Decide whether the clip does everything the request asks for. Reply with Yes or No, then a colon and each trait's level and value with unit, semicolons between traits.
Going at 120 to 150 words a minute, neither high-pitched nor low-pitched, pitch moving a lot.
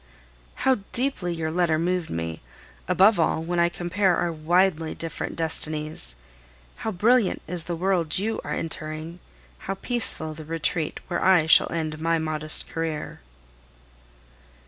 No: average, 140 wpm; medium, 165 Hz; narrow, 2.6 semitones